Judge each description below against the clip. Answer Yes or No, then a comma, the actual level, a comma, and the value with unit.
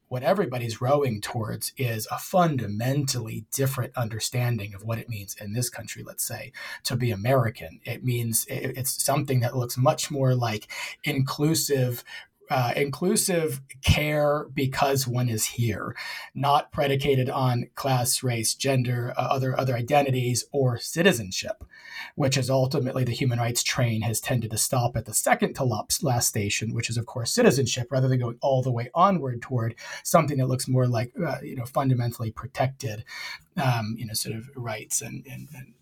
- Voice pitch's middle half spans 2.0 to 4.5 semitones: Yes, narrow, 2.6 semitones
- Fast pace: No, average, 165 wpm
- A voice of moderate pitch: No, low, 125 Hz